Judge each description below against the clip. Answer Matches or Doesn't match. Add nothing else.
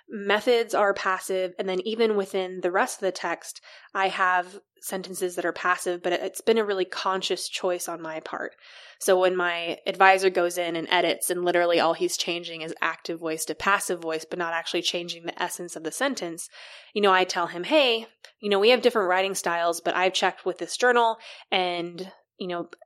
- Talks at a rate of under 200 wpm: Doesn't match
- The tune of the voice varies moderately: Doesn't match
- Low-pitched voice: Doesn't match